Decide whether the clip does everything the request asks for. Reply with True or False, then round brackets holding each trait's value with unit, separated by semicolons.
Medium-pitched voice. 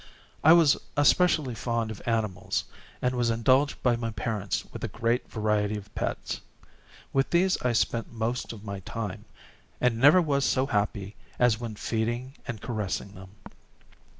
False (115 Hz)